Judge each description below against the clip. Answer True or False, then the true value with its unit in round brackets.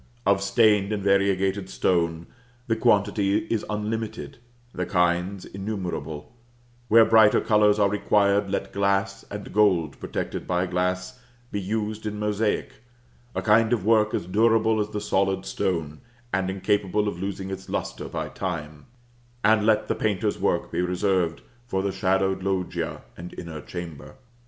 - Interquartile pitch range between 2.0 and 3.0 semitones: True (2.5 semitones)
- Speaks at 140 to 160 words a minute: True (145 wpm)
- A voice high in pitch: False (100 Hz)